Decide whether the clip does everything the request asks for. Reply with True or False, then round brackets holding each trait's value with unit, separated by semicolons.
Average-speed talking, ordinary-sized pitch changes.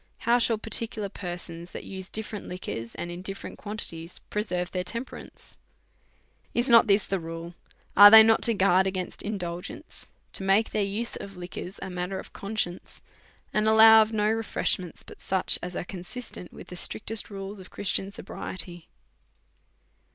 True (165 wpm; 3.3 semitones)